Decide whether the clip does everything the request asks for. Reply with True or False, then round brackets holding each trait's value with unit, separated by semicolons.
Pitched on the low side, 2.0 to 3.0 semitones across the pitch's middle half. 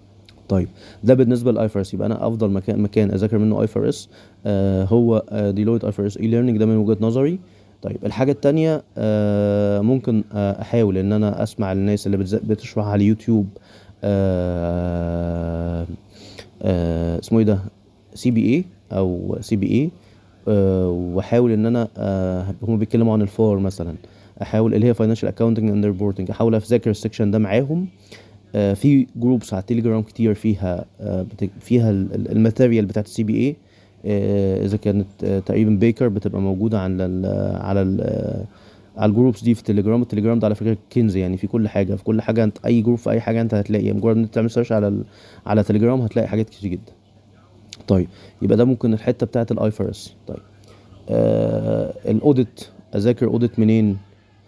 True (105 Hz; 2.4 semitones)